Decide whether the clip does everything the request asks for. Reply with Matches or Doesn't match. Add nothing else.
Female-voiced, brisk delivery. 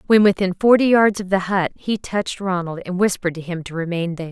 Matches